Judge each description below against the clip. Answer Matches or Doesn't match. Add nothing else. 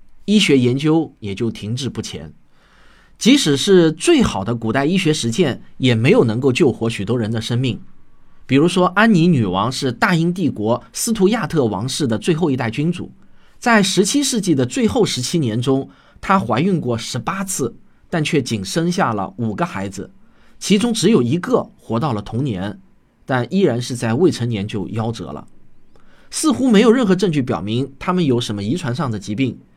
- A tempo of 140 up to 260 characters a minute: Doesn't match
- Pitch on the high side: Doesn't match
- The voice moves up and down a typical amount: Doesn't match